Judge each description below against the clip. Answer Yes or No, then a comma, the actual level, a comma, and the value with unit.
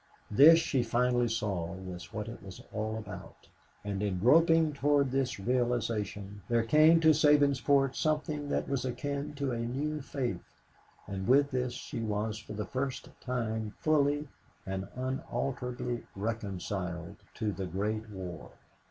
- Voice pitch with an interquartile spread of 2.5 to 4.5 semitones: No, average, 5.3 semitones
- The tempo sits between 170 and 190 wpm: No, average, 145 wpm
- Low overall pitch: Yes, low, 120 Hz